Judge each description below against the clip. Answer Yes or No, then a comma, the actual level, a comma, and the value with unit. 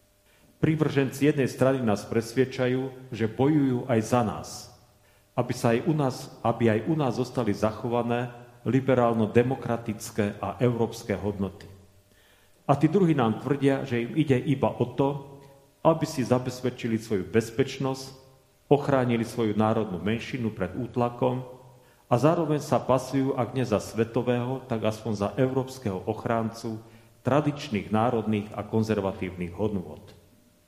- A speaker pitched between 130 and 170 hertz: No, low, 120 Hz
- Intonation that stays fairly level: No, average, 3.3 semitones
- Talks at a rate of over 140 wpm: No, average, 125 wpm